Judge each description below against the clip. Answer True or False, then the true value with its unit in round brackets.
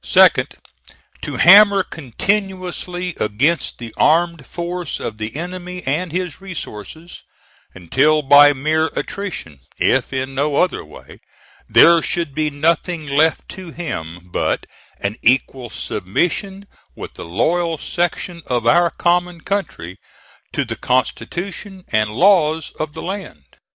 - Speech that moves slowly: True (125 wpm)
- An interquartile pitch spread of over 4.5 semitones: True (5.2 semitones)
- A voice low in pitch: False (160 Hz)